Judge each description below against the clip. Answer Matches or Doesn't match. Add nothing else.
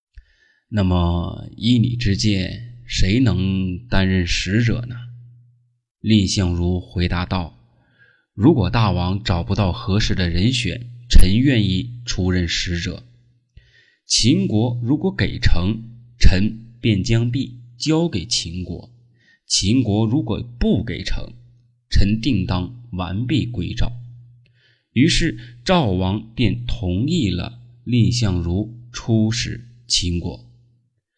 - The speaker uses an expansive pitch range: Doesn't match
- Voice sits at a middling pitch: Doesn't match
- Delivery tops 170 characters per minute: Doesn't match